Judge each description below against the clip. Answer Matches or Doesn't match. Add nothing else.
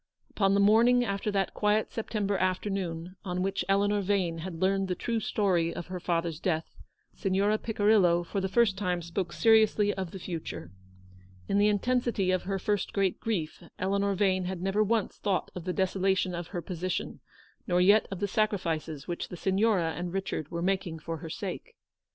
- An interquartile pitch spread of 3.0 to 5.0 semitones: Doesn't match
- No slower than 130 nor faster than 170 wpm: Doesn't match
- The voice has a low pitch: Doesn't match